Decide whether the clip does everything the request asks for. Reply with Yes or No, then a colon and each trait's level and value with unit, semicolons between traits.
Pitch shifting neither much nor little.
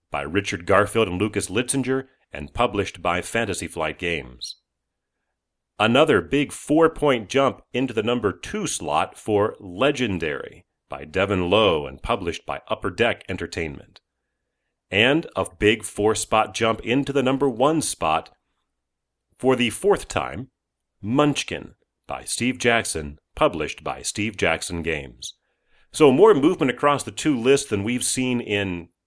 No: wide, 6.4 semitones